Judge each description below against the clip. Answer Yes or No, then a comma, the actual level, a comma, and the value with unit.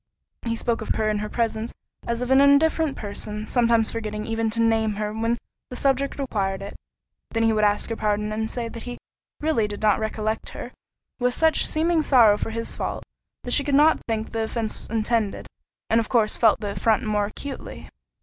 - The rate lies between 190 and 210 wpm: Yes, average, 200 wpm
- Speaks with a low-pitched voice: No, high, 225 Hz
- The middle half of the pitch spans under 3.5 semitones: Yes, narrow, 2.5 semitones